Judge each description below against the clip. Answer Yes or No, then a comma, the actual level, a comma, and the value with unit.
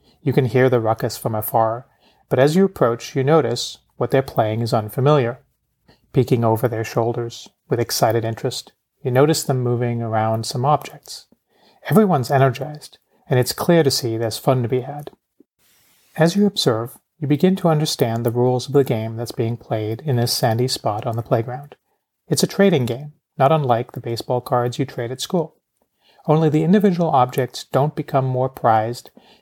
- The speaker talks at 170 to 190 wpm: Yes, average, 175 wpm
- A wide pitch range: No, average, 4.0 semitones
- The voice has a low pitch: Yes, low, 130 Hz